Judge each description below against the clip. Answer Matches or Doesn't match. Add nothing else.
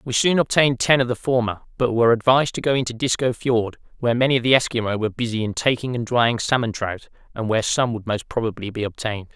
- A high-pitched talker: Doesn't match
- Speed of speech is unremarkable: Doesn't match